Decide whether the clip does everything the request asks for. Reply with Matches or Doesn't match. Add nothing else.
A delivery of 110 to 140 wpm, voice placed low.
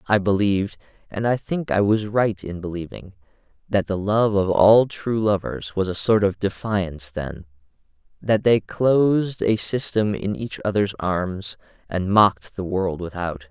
Doesn't match